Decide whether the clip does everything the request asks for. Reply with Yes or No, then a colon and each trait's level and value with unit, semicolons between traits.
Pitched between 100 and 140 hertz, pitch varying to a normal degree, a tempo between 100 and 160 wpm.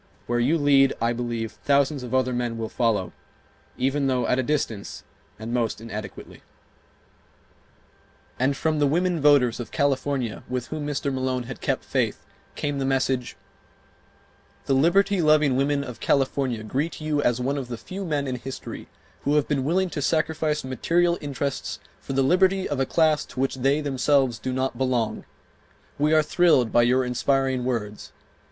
No: low, 135 Hz; average, 3.0 semitones; average, 170 wpm